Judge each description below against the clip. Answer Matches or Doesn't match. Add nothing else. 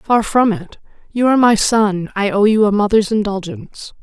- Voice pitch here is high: Matches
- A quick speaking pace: Doesn't match